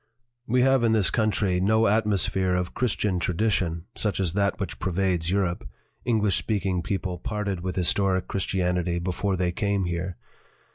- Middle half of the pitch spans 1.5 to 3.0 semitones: Yes, average, 2.7 semitones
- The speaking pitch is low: Yes, very low, 95 Hz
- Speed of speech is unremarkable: Yes, average, 155 wpm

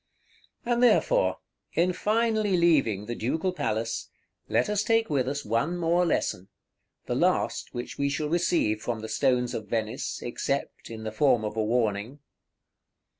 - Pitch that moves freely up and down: Yes, wide, 7.8 semitones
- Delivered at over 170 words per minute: No, average, 155 wpm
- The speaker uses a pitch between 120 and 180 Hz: Yes, low, 135 Hz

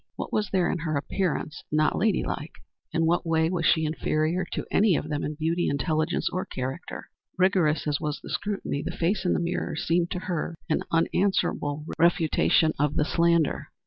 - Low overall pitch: No, medium, 165 Hz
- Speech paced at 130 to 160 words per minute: No, average, 190 wpm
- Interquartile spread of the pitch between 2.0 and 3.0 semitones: Yes, narrow, 2.6 semitones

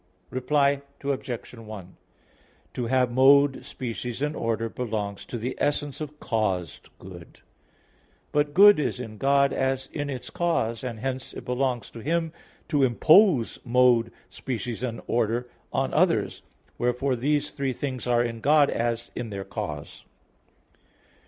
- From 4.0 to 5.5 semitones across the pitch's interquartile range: No, average, 3.4 semitones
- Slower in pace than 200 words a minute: Yes, average, 140 wpm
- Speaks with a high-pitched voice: No, low, 125 Hz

